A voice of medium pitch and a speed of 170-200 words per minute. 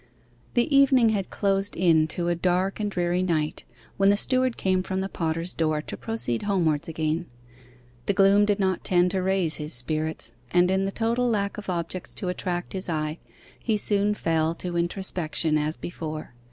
Yes: medium, 180 Hz; average, 180 wpm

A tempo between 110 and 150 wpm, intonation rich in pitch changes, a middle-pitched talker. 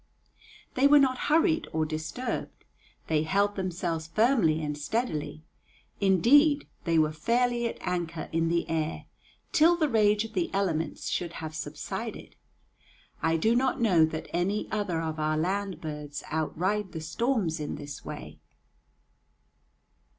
Yes: average, 140 wpm; wide, 6.2 semitones; medium, 175 Hz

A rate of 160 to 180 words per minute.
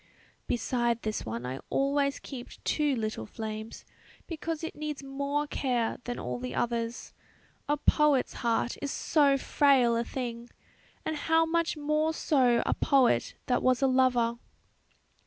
No: average, 145 wpm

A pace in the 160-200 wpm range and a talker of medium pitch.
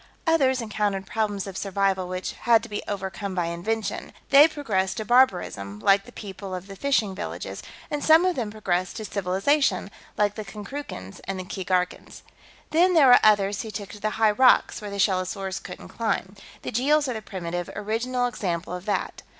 No: average, 185 wpm; high, 205 Hz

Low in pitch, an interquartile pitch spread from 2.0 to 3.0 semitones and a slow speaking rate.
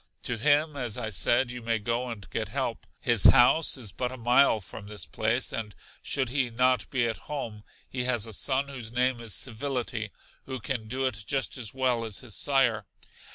No: low, 120 Hz; average, 2.7 semitones; average, 200 wpm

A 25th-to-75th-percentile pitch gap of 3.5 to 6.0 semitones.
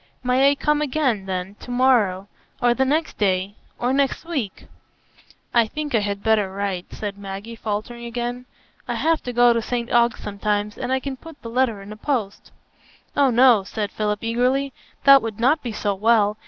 Yes: average, 4.1 semitones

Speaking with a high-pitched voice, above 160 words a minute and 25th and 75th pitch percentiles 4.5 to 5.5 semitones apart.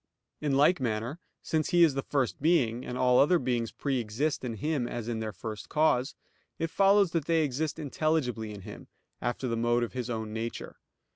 No: low, 130 Hz; average, 200 wpm; average, 5.1 semitones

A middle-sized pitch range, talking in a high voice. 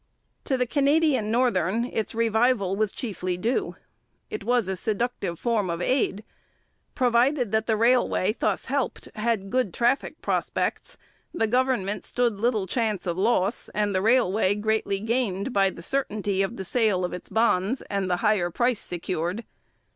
Yes: average, 4.1 semitones; high, 220 Hz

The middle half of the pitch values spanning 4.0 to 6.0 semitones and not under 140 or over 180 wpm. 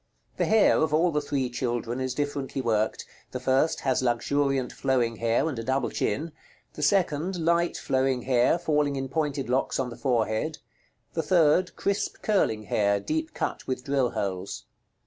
Yes: average, 4.3 semitones; average, 165 wpm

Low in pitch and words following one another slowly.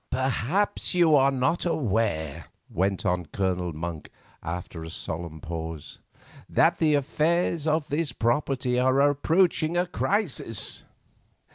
Yes: low, 130 Hz; slow, 120 wpm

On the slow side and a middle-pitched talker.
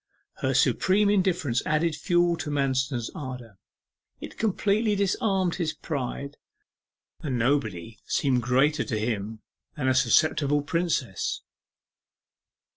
Yes: slow, 115 wpm; medium, 145 Hz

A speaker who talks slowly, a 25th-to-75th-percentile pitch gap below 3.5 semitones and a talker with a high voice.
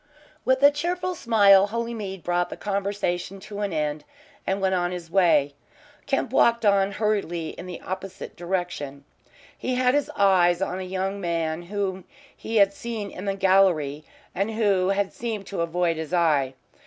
No: average, 165 wpm; average, 2.9 semitones; high, 195 Hz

